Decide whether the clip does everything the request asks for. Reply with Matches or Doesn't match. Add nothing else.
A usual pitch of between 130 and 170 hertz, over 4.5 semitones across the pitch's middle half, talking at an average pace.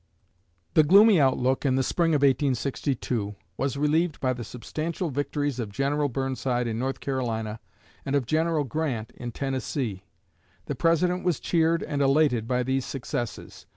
Doesn't match